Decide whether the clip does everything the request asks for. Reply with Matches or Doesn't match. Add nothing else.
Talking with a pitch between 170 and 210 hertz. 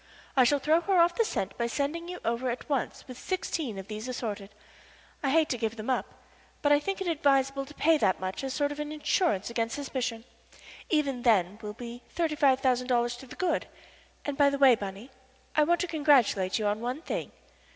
Doesn't match